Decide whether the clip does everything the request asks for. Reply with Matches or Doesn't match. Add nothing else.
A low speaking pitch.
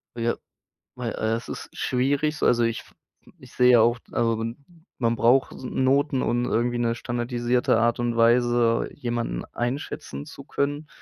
Matches